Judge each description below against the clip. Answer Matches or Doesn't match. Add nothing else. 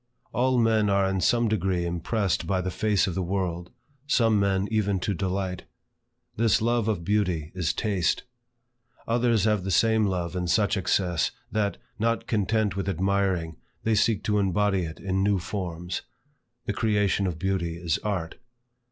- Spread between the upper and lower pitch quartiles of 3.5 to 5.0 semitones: Doesn't match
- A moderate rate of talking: Matches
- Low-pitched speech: Matches